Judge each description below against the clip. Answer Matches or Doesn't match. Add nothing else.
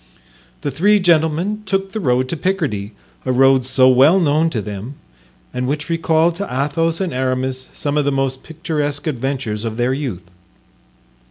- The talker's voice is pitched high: Doesn't match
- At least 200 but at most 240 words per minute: Doesn't match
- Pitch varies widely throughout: Doesn't match